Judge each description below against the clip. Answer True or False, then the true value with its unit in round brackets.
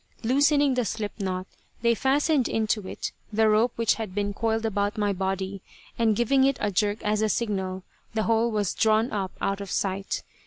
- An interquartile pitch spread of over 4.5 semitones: False (2.5 semitones)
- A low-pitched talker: False (215 Hz)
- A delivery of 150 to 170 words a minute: False (190 wpm)